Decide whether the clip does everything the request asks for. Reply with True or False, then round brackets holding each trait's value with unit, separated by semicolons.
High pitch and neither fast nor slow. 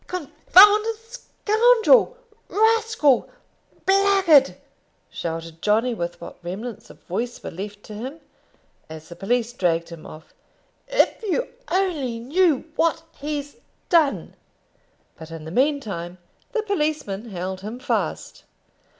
False (265 Hz; 120 wpm)